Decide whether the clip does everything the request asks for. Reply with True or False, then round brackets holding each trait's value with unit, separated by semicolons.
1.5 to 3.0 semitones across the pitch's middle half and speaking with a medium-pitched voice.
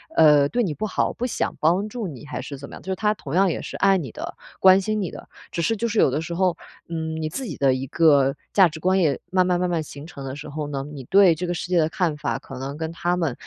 False (4.2 semitones; 165 Hz)